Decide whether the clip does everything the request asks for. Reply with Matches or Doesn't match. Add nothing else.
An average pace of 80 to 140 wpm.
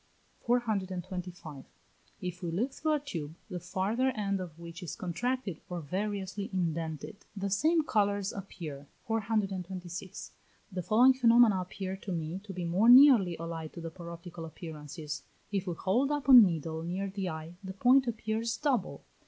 Doesn't match